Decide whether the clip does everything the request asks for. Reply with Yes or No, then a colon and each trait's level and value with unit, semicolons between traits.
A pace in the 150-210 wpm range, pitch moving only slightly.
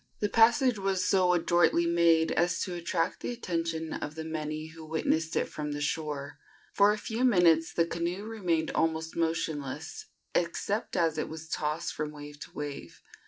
Yes: average, 170 wpm; narrow, 2.3 semitones